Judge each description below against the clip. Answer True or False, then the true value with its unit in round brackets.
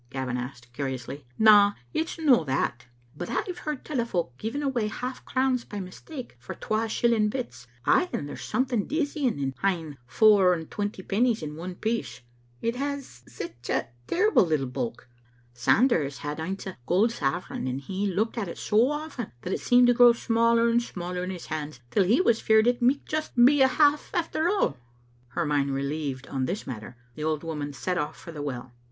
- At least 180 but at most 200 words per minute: True (195 wpm)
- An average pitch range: False (8.9 semitones)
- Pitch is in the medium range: False (195 Hz)